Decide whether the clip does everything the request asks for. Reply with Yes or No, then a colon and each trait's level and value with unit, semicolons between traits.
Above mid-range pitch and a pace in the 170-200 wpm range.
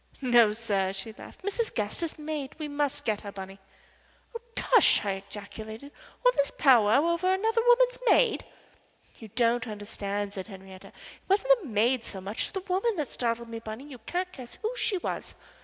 Yes: high, 245 Hz; average, 180 wpm